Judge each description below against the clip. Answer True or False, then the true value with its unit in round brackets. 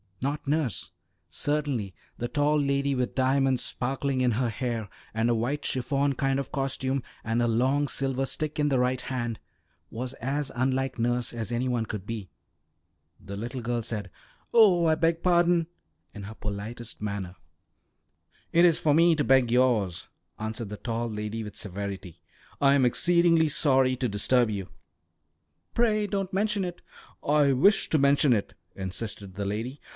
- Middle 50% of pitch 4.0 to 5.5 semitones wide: True (4.4 semitones)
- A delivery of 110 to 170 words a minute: True (160 wpm)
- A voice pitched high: False (130 Hz)